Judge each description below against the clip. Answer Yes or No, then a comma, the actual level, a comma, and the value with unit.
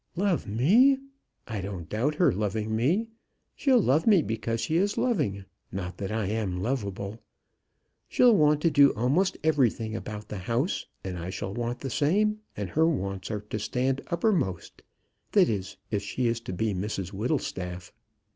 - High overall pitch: No, low, 115 Hz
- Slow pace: No, average, 165 wpm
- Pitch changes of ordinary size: No, wide, 7.8 semitones